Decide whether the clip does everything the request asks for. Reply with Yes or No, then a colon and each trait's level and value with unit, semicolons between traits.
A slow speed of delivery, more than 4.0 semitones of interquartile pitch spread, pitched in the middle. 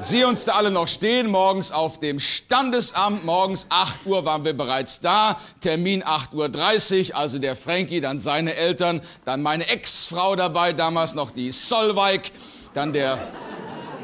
No: average, 155 wpm; average, 4.6 semitones; medium, 175 Hz